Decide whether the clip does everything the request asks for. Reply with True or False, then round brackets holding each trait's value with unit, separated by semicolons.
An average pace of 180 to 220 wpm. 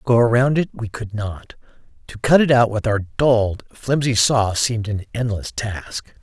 True (185 wpm)